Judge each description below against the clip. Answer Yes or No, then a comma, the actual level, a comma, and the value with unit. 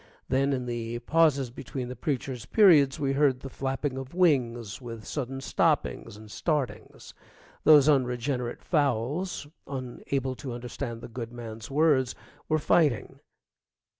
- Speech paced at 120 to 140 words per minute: Yes, slow, 135 wpm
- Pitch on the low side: Yes, low, 130 Hz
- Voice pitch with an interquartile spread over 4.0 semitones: No, average, 3.2 semitones